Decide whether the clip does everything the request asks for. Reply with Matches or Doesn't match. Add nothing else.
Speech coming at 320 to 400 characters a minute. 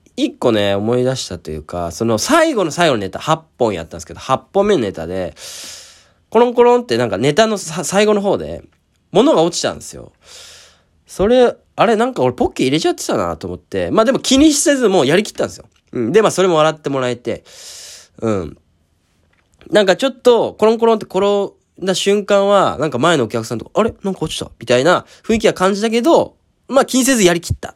Doesn't match